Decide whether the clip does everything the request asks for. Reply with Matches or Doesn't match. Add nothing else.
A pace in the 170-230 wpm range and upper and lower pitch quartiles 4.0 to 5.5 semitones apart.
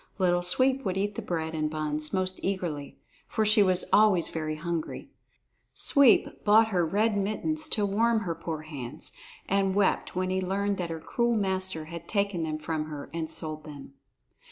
Matches